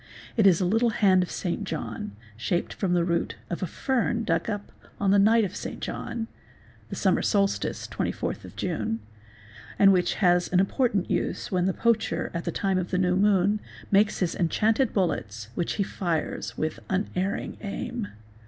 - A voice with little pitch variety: No, average, 3.0 semitones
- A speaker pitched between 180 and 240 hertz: Yes, high, 190 Hz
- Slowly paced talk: No, average, 175 wpm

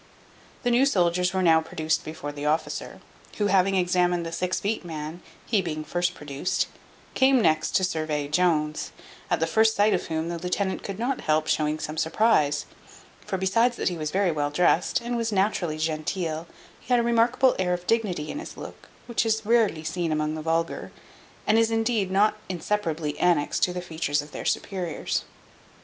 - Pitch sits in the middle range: Yes, medium, 180 Hz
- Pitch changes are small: No, average, 5.0 semitones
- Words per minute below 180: No, average, 185 wpm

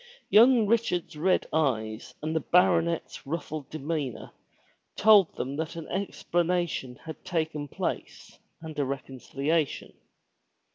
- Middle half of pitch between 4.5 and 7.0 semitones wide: No, average, 3.7 semitones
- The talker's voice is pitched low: No, medium, 160 Hz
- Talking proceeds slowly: Yes, slow, 110 wpm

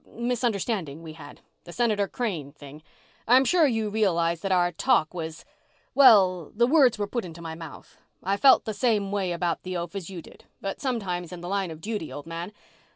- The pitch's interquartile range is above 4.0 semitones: Yes, average, 4.9 semitones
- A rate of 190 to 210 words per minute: Yes, average, 200 wpm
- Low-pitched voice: No, high, 190 Hz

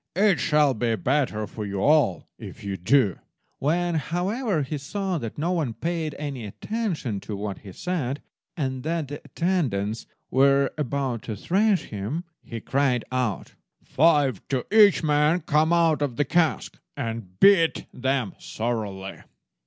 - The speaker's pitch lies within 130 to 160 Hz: Yes, medium, 140 Hz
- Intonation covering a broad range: Yes, wide, 6.5 semitones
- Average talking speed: Yes, average, 150 wpm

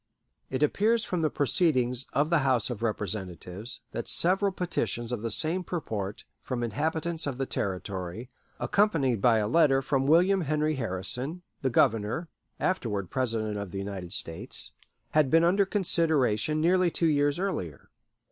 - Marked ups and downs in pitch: Yes, wide, 7.3 semitones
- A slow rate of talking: No, average, 150 wpm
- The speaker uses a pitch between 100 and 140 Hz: Yes, low, 135 Hz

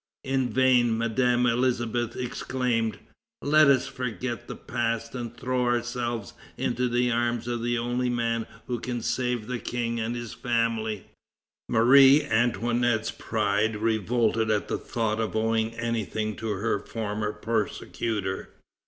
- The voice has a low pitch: Yes, low, 115 Hz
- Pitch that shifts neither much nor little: No, narrow, 1.7 semitones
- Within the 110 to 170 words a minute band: Yes, slow, 135 wpm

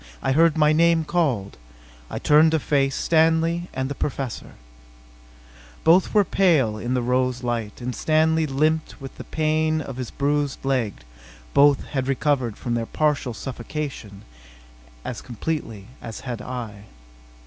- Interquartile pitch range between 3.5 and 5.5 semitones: Yes, average, 4.3 semitones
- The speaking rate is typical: Yes, average, 150 wpm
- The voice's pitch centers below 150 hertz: Yes, medium, 140 Hz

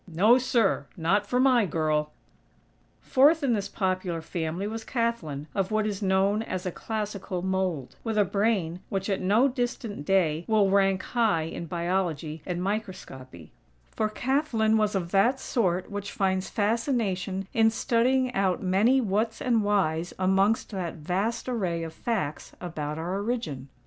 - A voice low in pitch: No, high, 195 Hz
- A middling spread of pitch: Yes, average, 4.1 semitones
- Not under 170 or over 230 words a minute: No, average, 155 wpm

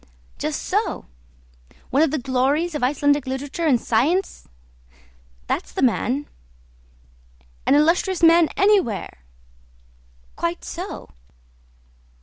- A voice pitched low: No, very high, 295 Hz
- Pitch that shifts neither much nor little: Yes, average, 4.4 semitones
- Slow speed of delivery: Yes, slow, 100 wpm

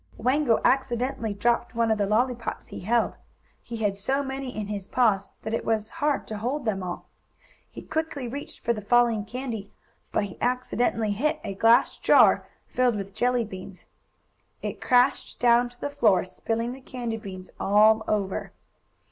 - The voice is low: No, high, 230 Hz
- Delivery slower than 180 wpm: Yes, average, 170 wpm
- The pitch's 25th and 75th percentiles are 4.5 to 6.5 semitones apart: No, average, 3.2 semitones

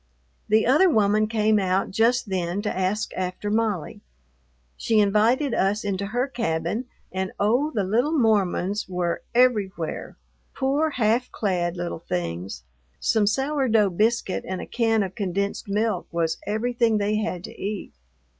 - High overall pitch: Yes, high, 210 Hz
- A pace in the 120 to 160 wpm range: Yes, average, 145 wpm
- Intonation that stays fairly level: No, average, 3.5 semitones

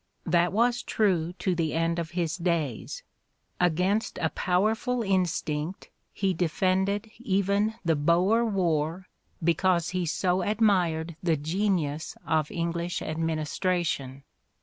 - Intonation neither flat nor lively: Yes, average, 3.2 semitones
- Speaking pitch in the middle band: Yes, medium, 175 Hz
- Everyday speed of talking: No, slow, 115 wpm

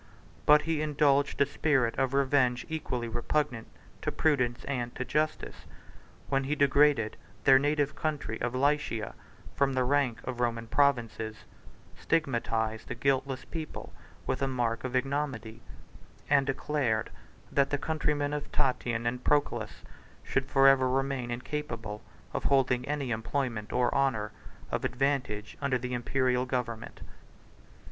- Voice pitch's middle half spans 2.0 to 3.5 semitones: Yes, average, 3.0 semitones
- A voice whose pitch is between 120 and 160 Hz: Yes, low, 135 Hz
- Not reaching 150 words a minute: Yes, slow, 135 wpm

